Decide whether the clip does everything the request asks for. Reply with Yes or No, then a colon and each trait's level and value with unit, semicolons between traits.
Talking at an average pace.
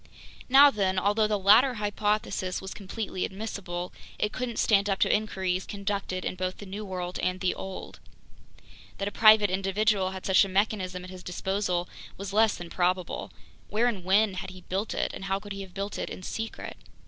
Yes: average, 195 wpm